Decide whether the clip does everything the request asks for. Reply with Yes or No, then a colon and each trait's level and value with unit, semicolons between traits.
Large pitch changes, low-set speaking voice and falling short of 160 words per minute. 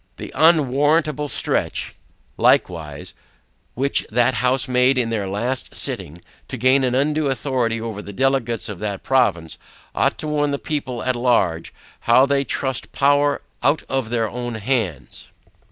No: average, 3.7 semitones; low, 125 Hz; average, 150 wpm